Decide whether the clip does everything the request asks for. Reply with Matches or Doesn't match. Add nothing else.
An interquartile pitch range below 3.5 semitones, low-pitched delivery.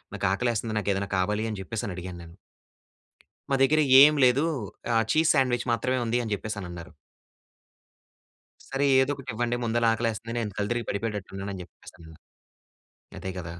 Doesn't match